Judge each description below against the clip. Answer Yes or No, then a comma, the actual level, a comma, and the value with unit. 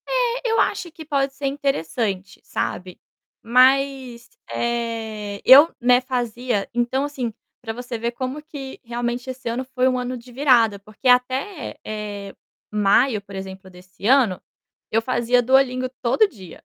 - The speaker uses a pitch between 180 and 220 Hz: No, high, 245 Hz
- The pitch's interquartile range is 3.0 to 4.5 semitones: Yes, average, 3.5 semitones